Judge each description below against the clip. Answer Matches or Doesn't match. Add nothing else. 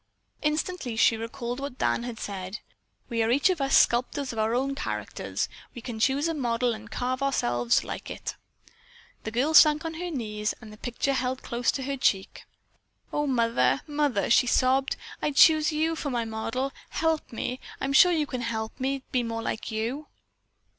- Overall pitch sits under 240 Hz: Doesn't match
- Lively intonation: Doesn't match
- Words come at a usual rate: Matches